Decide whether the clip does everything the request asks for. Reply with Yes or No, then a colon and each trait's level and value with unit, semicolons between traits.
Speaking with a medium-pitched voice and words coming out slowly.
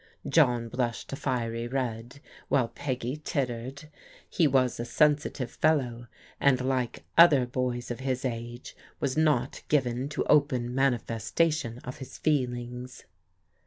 No: low, 130 Hz; slow, 125 wpm